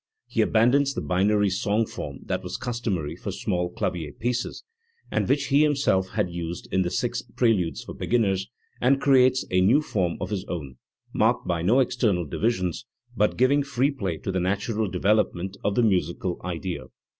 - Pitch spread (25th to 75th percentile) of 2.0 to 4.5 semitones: No, average, 5.3 semitones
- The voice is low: Yes, low, 100 Hz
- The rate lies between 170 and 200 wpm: Yes, average, 175 wpm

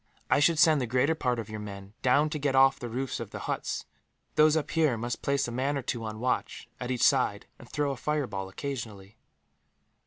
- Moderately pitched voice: No, low, 130 Hz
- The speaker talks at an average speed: No, fast, 220 wpm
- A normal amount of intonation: Yes, average, 4.0 semitones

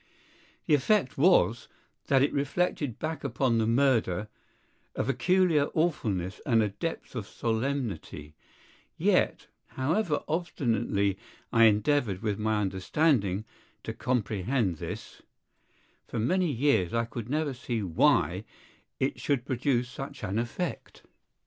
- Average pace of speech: No, slow, 120 wpm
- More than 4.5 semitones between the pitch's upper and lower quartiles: Yes, average, 5.2 semitones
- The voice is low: Yes, low, 125 Hz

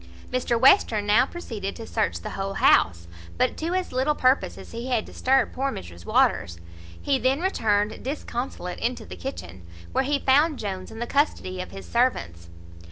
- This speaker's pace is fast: No, average, 175 wpm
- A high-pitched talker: Yes, high, 235 Hz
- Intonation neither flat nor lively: No, wide, 6.2 semitones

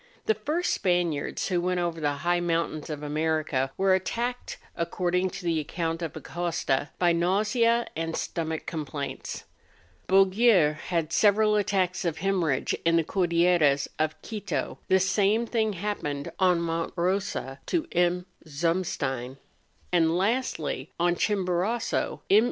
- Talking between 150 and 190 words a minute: No, average, 140 wpm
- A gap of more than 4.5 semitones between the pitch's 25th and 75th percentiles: No, average, 3.3 semitones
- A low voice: No, medium, 175 Hz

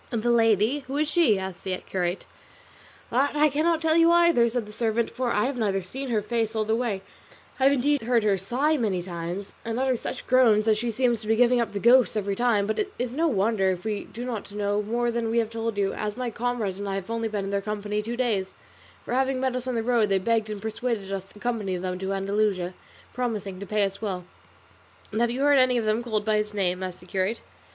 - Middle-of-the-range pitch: No, high, 220 Hz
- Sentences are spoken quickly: Yes, fast, 250 wpm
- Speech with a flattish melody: No, average, 3.5 semitones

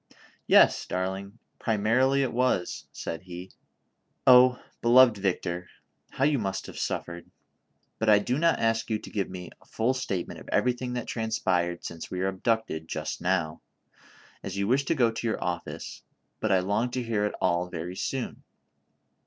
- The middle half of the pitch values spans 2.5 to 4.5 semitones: No, average, 5.1 semitones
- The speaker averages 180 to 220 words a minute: No, average, 170 wpm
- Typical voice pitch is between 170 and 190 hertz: No, low, 105 Hz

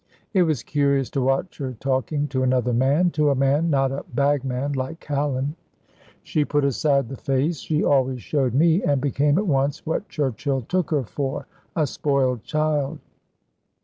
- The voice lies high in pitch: No, medium, 140 Hz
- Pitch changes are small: Yes, narrow, 2.2 semitones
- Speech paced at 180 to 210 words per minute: No, average, 170 wpm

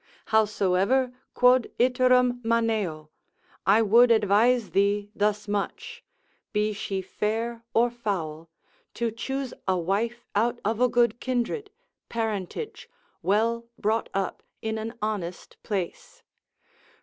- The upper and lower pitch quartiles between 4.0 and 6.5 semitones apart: No, average, 2.9 semitones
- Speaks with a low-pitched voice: No, high, 220 Hz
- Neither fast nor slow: No, slow, 115 wpm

